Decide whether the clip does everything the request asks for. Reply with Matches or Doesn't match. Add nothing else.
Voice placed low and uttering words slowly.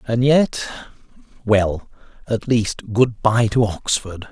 Matches